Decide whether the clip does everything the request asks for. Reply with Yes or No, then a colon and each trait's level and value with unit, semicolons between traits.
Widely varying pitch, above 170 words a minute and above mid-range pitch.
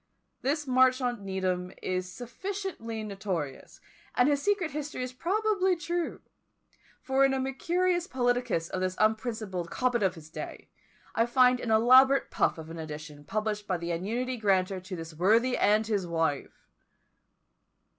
No: wide, 6.2 semitones; average, 145 wpm; high, 225 Hz